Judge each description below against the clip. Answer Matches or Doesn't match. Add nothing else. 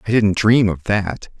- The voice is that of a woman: Doesn't match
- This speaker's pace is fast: Matches